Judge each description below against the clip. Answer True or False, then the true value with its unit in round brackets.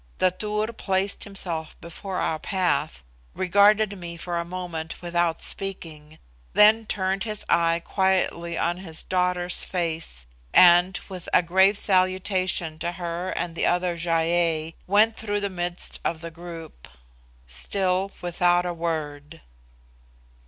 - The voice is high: False (175 Hz)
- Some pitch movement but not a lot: False (2.2 semitones)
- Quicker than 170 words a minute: False (135 wpm)